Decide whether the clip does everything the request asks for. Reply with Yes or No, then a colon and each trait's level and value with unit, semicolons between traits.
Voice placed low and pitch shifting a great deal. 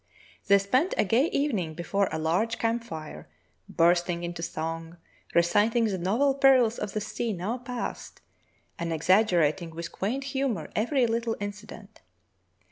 No: high, 205 Hz; wide, 5.7 semitones